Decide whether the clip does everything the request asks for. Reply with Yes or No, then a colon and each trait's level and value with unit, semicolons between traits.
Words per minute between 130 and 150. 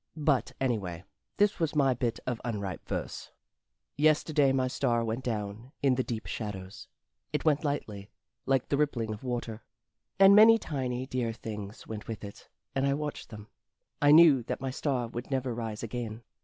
No: average, 170 wpm